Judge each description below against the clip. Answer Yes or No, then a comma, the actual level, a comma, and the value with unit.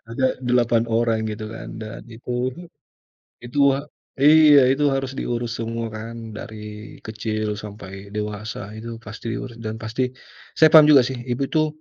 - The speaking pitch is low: Yes, low, 115 Hz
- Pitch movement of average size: Yes, average, 3.1 semitones